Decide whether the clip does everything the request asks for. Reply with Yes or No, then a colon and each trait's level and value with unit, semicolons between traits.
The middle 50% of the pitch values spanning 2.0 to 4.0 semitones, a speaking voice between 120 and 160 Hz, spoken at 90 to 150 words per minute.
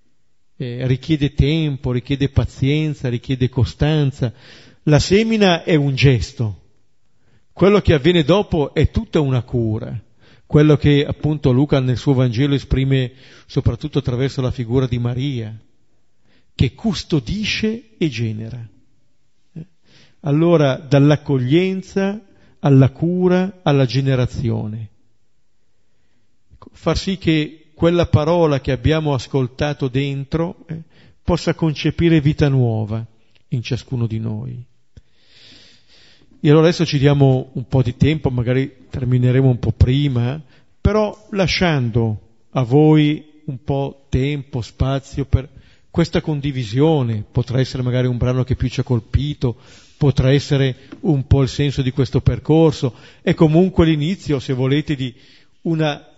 Yes: average, 3.6 semitones; low, 135 Hz; average, 120 wpm